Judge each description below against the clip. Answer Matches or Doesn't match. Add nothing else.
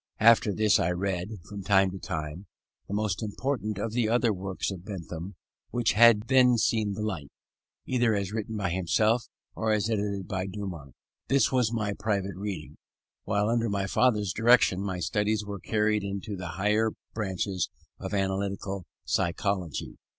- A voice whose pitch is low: Matches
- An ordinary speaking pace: Matches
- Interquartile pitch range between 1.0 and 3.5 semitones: Matches